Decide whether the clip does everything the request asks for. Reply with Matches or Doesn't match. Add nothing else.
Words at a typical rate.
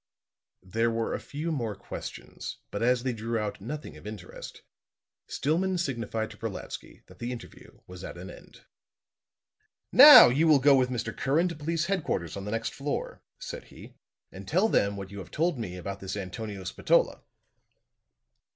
Matches